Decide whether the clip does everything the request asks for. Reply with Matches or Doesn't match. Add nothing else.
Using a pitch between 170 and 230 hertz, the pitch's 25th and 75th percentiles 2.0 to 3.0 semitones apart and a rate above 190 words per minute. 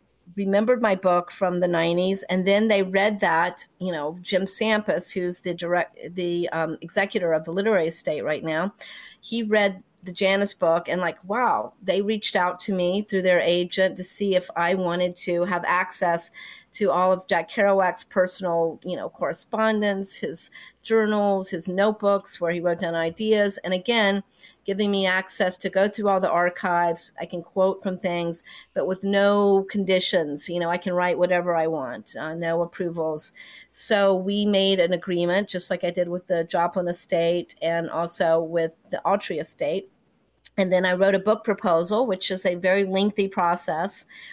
Doesn't match